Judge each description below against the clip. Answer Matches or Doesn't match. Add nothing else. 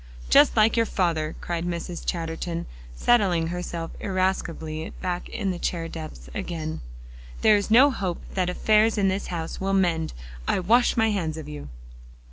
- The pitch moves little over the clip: Doesn't match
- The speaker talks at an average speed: Matches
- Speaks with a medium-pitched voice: Matches